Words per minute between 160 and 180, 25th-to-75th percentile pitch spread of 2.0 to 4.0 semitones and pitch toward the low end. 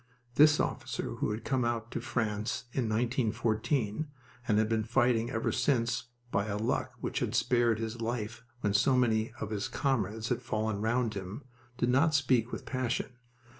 Yes: average, 170 wpm; narrow, 2.5 semitones; low, 115 Hz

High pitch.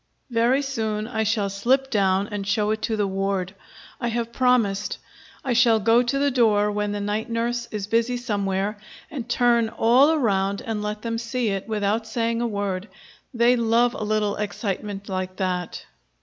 Yes: high, 220 Hz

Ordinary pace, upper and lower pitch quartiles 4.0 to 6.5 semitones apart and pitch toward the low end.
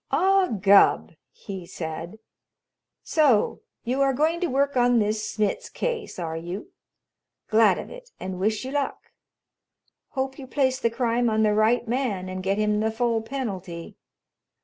No: average, 155 wpm; average, 5.1 semitones; high, 225 Hz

